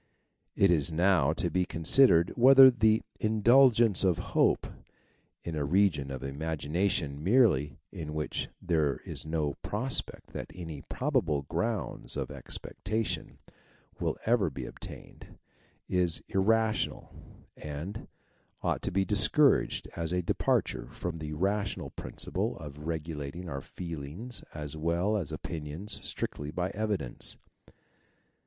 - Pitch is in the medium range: No, very low, 85 Hz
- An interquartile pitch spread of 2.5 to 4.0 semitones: No, wide, 5.6 semitones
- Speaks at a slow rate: Yes, slow, 120 wpm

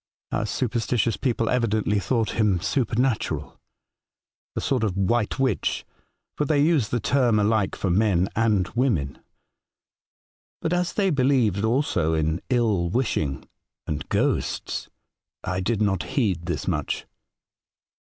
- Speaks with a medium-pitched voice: No, low, 110 Hz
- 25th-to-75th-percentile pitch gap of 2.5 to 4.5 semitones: No, average, 5.1 semitones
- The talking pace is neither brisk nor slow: No, slow, 130 wpm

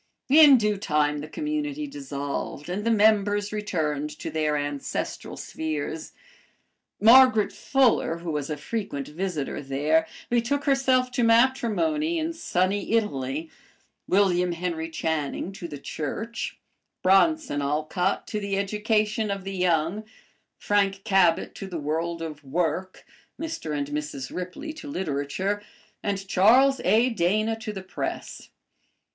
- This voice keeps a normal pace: No, slow, 130 wpm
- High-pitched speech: Yes, high, 195 Hz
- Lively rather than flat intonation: Yes, wide, 6.4 semitones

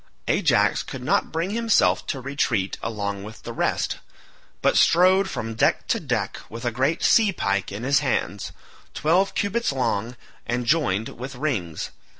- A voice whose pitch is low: Yes, low, 130 Hz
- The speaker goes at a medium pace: Yes, average, 155 wpm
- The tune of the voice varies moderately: No, wide, 7.2 semitones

